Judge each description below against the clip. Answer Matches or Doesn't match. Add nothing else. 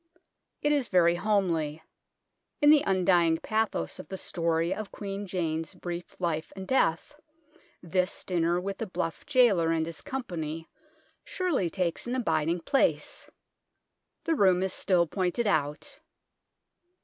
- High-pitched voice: Doesn't match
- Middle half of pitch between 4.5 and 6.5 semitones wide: Doesn't match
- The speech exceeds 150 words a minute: Doesn't match